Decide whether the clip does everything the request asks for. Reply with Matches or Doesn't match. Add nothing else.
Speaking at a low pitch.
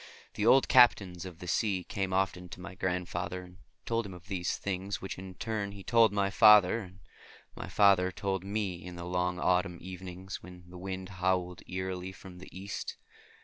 Matches